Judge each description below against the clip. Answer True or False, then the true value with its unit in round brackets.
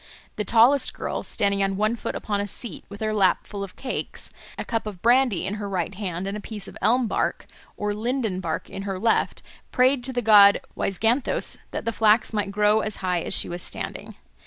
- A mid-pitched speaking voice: False (210 Hz)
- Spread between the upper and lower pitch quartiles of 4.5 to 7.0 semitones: False (2.7 semitones)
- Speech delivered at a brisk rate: True (215 wpm)